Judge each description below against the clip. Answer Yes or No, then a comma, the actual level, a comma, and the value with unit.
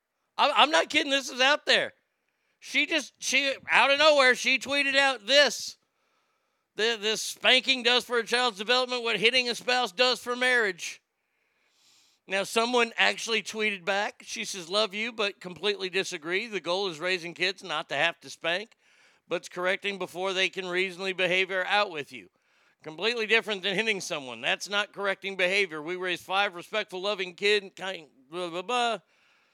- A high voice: Yes, high, 205 Hz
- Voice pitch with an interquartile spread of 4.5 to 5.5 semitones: Yes, average, 4.9 semitones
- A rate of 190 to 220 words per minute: No, average, 175 wpm